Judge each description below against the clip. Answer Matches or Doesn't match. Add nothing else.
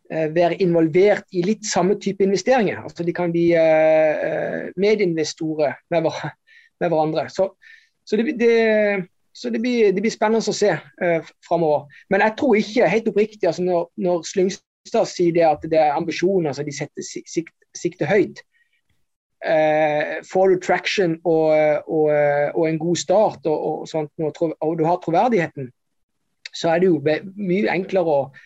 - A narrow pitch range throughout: Doesn't match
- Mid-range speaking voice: Matches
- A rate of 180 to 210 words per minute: Doesn't match